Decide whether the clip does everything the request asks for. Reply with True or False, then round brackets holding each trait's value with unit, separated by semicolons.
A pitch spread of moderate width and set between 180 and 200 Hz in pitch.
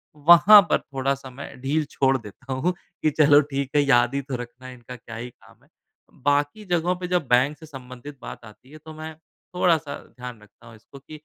False (3.7 semitones; 140 Hz)